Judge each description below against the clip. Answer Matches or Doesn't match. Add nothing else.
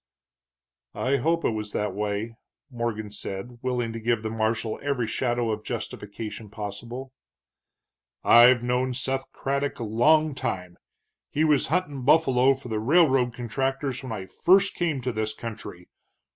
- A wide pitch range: Doesn't match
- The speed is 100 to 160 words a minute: Matches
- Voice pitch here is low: Matches